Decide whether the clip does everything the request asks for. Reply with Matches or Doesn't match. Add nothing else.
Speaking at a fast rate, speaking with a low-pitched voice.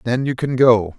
Matches